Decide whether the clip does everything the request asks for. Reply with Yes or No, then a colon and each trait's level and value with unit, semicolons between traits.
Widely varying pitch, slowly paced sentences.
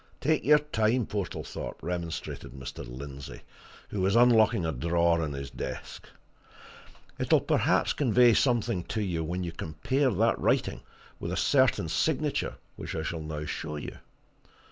No: wide, 6.8 semitones; average, 145 wpm